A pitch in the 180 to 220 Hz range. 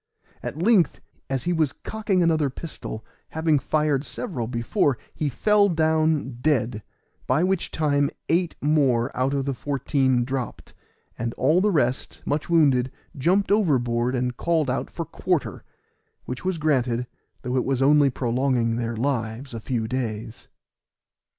No: medium, 140 Hz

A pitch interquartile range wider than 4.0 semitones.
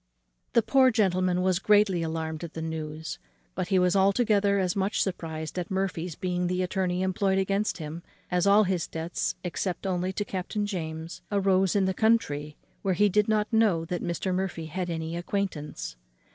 No: average, 3.0 semitones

